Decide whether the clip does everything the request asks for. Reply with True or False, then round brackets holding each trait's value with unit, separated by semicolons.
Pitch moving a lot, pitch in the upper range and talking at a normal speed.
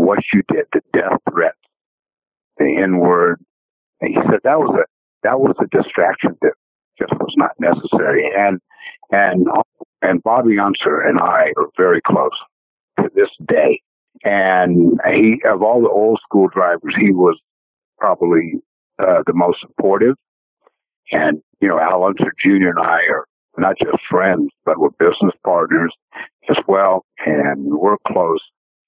True (7.3 semitones; 390 Hz; 150 wpm)